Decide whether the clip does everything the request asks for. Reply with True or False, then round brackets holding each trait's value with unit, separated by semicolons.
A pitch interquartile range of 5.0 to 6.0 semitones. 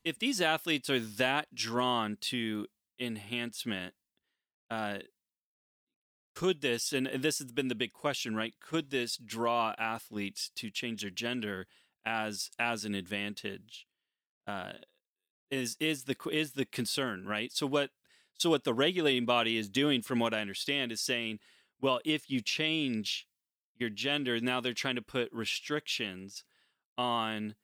False (3.7 semitones)